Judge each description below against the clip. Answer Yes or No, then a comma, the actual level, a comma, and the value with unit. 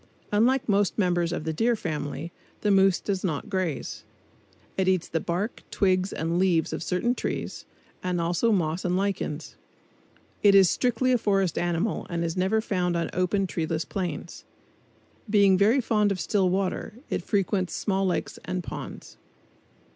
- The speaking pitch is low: No, medium, 185 Hz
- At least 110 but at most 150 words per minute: No, average, 160 wpm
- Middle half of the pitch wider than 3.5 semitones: No, average, 2.8 semitones